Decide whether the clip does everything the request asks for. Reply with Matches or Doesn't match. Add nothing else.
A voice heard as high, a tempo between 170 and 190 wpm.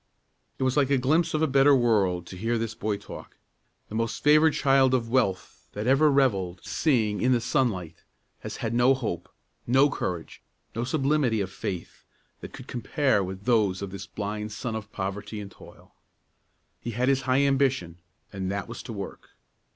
Doesn't match